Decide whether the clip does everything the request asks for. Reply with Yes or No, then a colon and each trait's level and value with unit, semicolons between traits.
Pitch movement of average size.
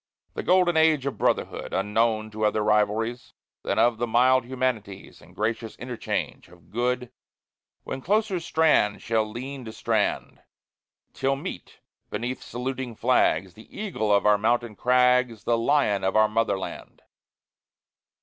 Yes: average, 3.3 semitones